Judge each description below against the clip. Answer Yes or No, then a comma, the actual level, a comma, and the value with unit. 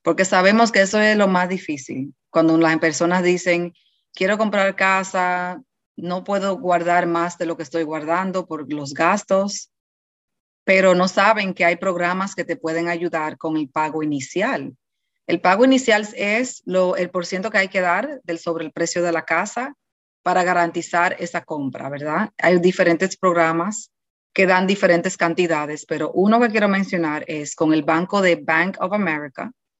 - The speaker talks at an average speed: Yes, average, 170 wpm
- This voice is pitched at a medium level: Yes, medium, 180 Hz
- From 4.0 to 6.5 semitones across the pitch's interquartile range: No, average, 2.8 semitones